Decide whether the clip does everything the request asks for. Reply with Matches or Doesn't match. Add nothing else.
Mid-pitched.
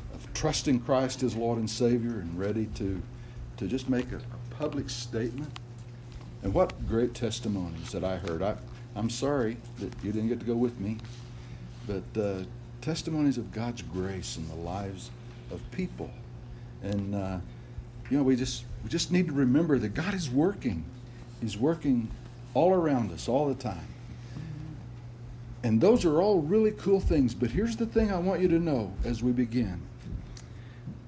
Doesn't match